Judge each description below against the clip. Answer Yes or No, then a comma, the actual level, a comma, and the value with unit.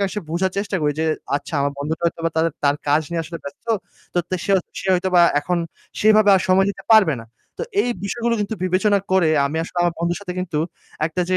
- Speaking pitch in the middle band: Yes, medium, 180 Hz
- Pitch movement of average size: Yes, average, 3.6 semitones